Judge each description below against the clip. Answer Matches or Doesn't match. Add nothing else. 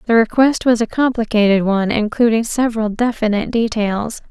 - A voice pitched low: Doesn't match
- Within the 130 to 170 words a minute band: Matches